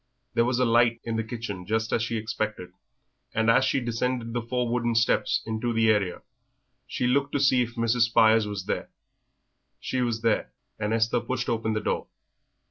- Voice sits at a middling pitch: No, low, 115 Hz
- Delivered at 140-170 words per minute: No, average, 190 wpm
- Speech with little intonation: Yes, narrow, 1.6 semitones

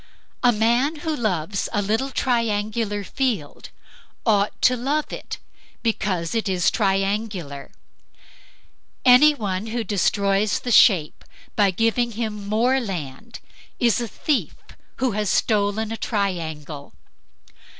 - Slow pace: Yes, slow, 115 wpm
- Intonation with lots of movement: No, average, 3.4 semitones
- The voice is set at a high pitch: Yes, high, 215 Hz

